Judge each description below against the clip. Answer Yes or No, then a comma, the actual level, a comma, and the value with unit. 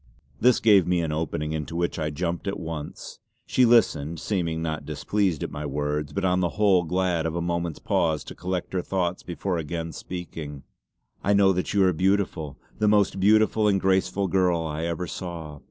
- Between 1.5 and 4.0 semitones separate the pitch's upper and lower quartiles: Yes, average, 3.2 semitones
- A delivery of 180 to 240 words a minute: Yes, average, 190 wpm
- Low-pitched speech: Yes, very low, 85 Hz